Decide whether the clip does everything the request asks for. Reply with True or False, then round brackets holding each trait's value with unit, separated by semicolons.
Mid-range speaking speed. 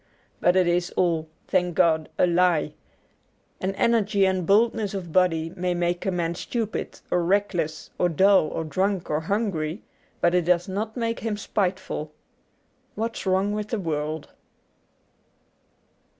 True (145 wpm)